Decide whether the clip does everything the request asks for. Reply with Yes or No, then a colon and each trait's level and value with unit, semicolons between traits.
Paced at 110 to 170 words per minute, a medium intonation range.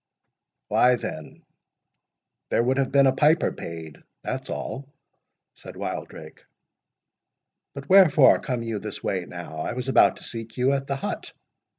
Yes: average, 140 wpm; average, 3.3 semitones